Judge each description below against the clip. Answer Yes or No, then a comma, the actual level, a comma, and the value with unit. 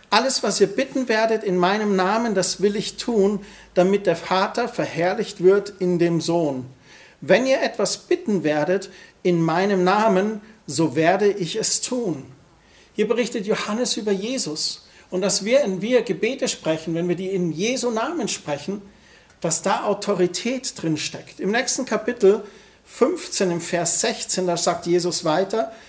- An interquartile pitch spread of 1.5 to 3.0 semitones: No, average, 3.9 semitones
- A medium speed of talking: Yes, average, 160 wpm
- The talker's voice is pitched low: No, high, 195 Hz